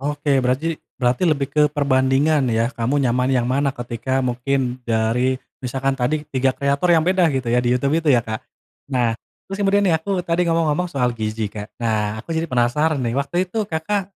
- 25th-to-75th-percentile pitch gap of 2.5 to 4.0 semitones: No, average, 4.5 semitones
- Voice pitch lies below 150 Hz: Yes, low, 135 Hz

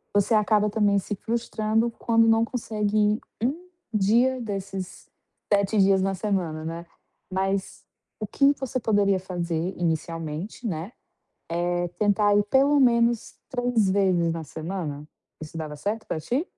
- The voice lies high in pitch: Yes, high, 200 Hz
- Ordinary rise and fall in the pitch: Yes, average, 4.3 semitones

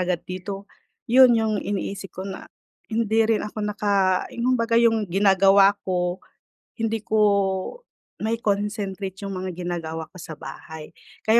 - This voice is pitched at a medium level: No, high, 200 Hz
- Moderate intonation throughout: Yes, average, 3.1 semitones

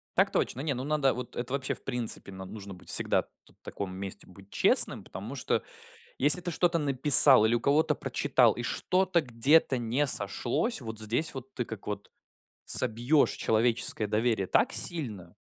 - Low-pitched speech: Yes, low, 125 Hz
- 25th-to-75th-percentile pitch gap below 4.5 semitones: No, average, 5.0 semitones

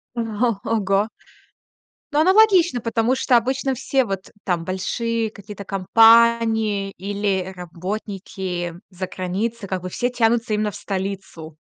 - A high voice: Yes, high, 210 Hz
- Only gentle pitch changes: No, average, 3.6 semitones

